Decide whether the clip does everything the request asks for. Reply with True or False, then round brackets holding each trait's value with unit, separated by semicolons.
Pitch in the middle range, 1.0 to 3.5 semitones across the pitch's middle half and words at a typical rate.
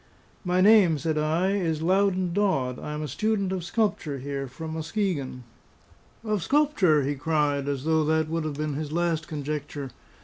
False (160 Hz; 4.2 semitones; 170 wpm)